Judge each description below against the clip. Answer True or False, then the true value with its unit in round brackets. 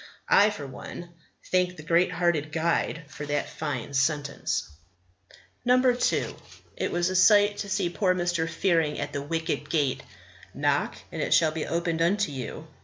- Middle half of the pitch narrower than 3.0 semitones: False (3.6 semitones)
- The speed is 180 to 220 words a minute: False (160 wpm)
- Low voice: False (165 Hz)